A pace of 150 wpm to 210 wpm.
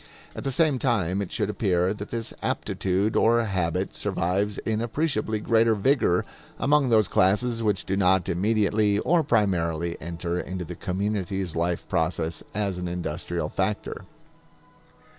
No: average, 140 wpm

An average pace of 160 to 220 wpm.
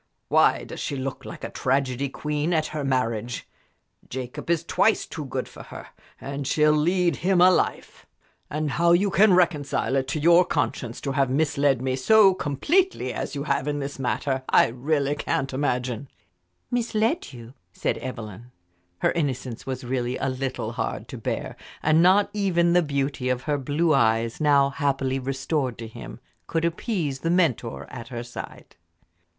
Yes: average, 170 wpm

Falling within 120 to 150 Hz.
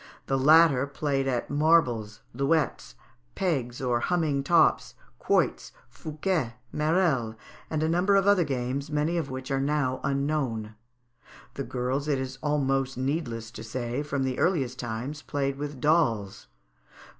Yes: medium, 140 Hz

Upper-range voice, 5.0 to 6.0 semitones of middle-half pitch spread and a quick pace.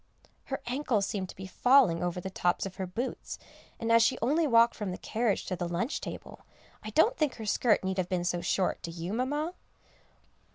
Yes: high, 210 Hz; wide, 5.4 semitones; fast, 210 wpm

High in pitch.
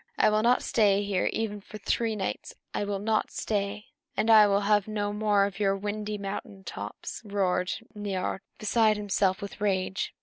Yes: high, 205 Hz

